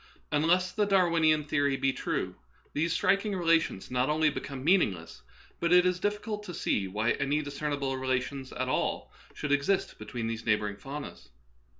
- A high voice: No, medium, 145 Hz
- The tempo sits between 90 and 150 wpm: No, average, 160 wpm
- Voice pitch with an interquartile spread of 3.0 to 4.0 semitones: No, average, 5.0 semitones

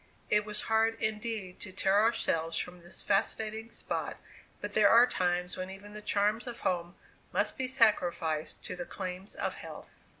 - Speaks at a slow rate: No, average, 170 wpm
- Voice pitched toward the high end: Yes, high, 205 Hz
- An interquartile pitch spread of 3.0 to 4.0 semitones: Yes, average, 3.5 semitones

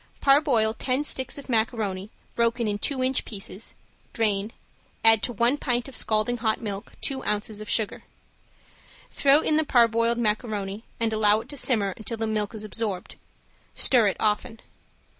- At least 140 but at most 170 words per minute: Yes, average, 160 wpm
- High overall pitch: Yes, high, 225 Hz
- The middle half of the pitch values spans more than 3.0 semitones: No, average, 2.7 semitones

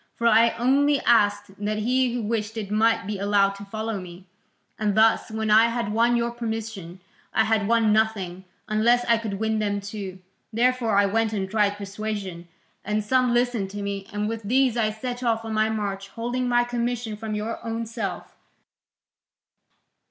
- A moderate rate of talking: Yes, average, 180 wpm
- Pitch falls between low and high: No, high, 220 Hz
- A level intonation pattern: Yes, narrow, 2.3 semitones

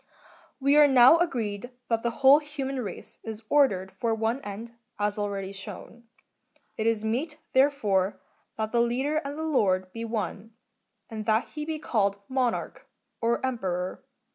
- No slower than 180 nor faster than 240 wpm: No, average, 150 wpm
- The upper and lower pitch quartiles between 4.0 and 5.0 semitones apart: Yes, average, 4.7 semitones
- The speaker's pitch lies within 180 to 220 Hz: No, high, 230 Hz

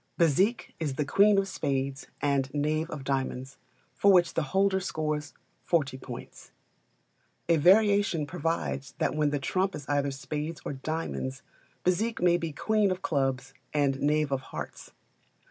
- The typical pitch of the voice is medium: Yes, medium, 150 Hz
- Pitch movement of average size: Yes, average, 4.6 semitones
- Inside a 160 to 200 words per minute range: No, average, 150 wpm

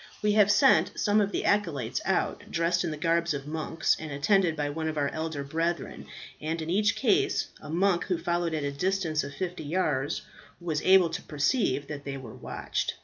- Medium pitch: Yes, medium, 165 Hz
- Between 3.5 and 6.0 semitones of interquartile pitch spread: Yes, average, 4.0 semitones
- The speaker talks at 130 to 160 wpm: No, fast, 205 wpm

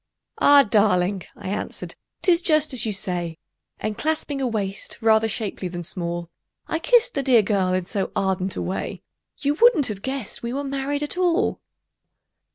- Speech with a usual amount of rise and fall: No, wide, 7.0 semitones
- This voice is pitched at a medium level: No, high, 225 Hz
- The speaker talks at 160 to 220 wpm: Yes, average, 170 wpm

